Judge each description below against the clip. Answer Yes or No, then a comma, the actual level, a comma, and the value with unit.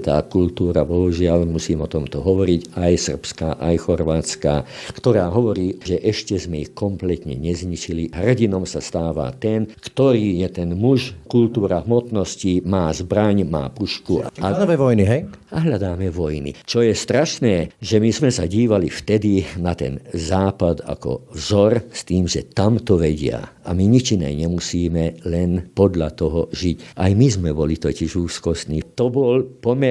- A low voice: Yes, very low, 90 Hz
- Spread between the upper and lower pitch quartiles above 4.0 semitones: Yes, average, 4.6 semitones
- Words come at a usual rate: Yes, average, 155 wpm